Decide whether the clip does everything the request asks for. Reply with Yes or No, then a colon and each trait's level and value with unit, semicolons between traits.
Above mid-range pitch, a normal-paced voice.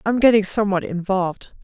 Yes: high, 200 Hz; average, 145 wpm